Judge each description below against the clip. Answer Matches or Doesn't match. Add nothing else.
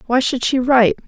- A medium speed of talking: Doesn't match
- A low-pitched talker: Doesn't match